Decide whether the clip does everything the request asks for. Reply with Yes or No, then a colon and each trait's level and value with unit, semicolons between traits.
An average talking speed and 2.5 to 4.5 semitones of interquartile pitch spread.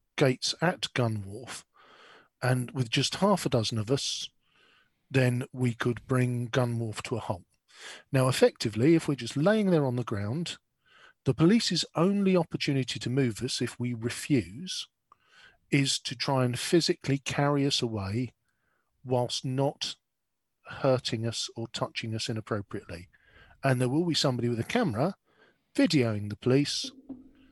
Yes: average, 150 wpm; average, 3.8 semitones